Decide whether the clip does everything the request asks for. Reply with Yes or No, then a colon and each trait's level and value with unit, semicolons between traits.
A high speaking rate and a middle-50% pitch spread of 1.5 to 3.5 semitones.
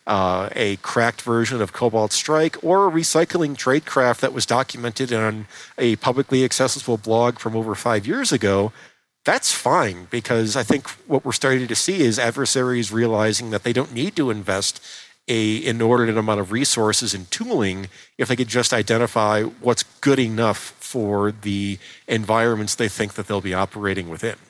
No: average, 165 wpm; average, 3.0 semitones